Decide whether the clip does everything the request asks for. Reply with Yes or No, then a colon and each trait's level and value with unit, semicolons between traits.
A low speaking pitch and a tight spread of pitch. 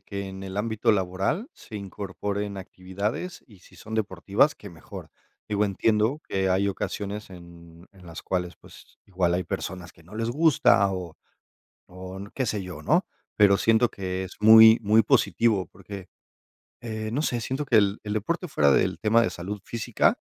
No: low, 100 Hz; average, 3.1 semitones